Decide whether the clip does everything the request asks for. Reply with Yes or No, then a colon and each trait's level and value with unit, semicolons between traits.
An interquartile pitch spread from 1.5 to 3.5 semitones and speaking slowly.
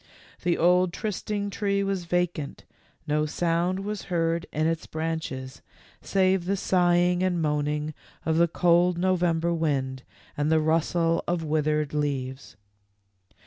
No: average, 2.7 semitones; average, 145 wpm